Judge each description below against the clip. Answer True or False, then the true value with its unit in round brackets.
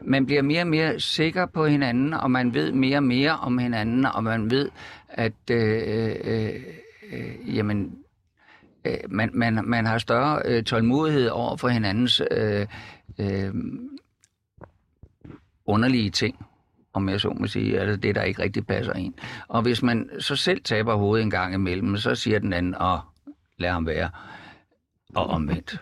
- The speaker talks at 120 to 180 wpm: True (165 wpm)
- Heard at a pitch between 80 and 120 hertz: True (115 Hz)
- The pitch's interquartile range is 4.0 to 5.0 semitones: True (4.5 semitones)